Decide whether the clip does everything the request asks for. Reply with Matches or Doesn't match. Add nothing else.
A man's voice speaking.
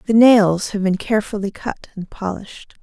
Doesn't match